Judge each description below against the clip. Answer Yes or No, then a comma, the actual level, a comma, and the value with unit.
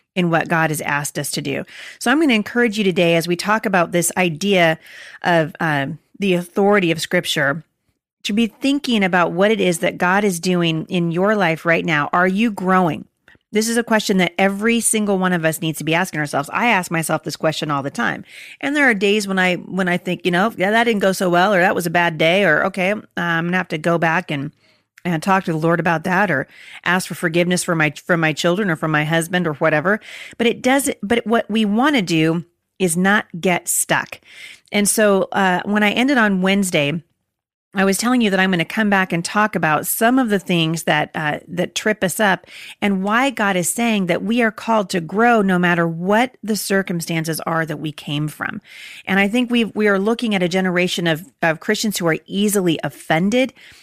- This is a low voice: No, medium, 185 Hz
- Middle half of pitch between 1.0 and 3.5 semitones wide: No, average, 4.2 semitones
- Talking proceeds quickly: Yes, fast, 230 wpm